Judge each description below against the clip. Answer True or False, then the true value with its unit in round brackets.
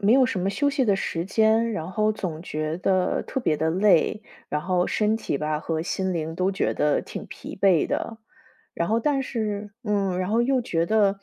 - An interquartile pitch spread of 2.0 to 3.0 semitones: False (4.6 semitones)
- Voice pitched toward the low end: False (195 Hz)